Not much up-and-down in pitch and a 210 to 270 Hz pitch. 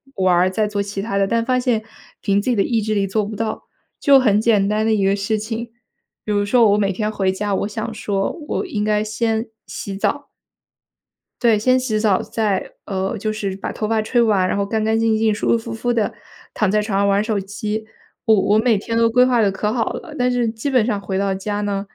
Yes: narrow, 2.1 semitones; high, 215 Hz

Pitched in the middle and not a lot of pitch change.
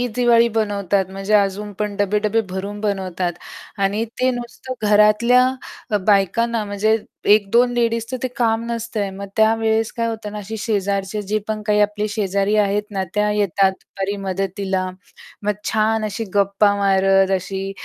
No: high, 210 Hz; narrow, 2.1 semitones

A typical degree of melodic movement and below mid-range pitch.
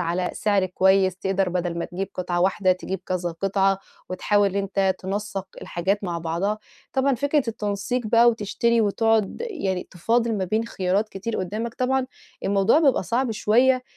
No: average, 3.6 semitones; high, 200 Hz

